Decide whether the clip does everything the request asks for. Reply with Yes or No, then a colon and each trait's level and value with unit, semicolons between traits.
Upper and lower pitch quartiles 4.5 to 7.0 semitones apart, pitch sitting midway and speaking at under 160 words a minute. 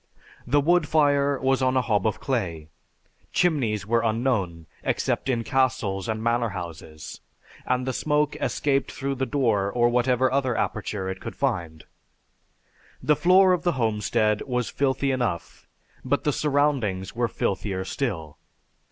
No: average, 5.3 semitones; low, 125 Hz; average, 145 wpm